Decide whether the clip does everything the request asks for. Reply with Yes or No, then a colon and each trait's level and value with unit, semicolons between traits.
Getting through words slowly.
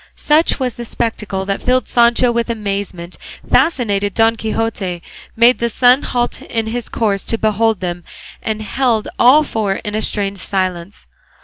No: average, 155 wpm